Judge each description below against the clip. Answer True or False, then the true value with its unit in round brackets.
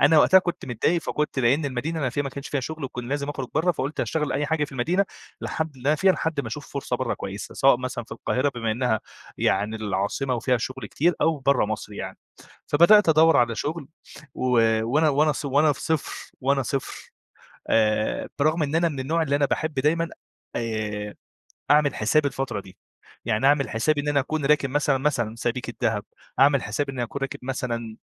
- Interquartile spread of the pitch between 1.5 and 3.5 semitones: False (4.0 semitones)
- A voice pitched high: False (140 Hz)